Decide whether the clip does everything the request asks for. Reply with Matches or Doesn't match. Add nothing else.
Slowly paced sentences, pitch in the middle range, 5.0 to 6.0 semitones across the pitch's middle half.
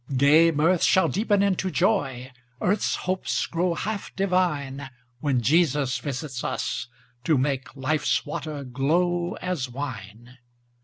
Matches